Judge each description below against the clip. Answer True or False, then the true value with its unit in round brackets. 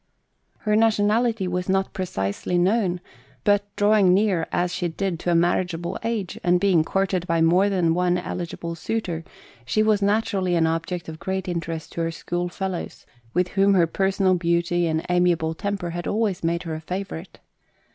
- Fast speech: False (165 wpm)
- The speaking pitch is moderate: True (180 Hz)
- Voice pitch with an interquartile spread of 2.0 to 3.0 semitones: True (2.7 semitones)